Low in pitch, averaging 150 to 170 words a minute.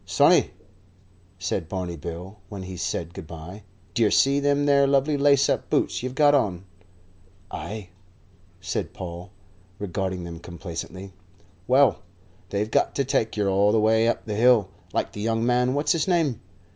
Yes: low, 105 Hz; average, 160 wpm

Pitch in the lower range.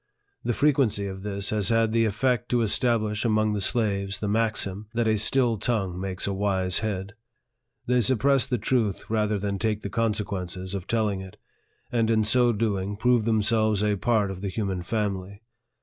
Yes: low, 105 Hz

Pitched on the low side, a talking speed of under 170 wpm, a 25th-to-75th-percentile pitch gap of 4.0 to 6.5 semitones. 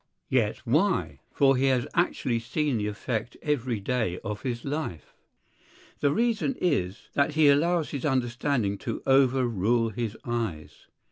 Yes: low, 125 Hz; average, 140 wpm; average, 4.3 semitones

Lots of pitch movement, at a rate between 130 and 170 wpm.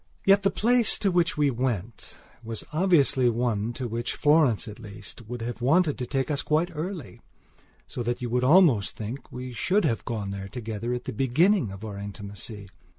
No: wide, 5.8 semitones; average, 190 wpm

